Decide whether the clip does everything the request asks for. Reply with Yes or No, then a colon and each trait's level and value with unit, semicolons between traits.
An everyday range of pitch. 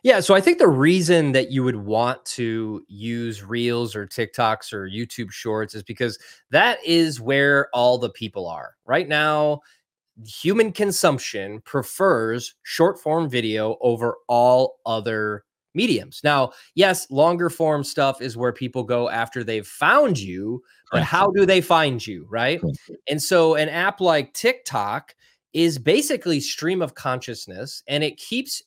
No: wide, 6.3 semitones